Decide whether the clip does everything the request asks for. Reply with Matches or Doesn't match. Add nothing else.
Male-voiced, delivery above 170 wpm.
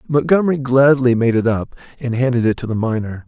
Matches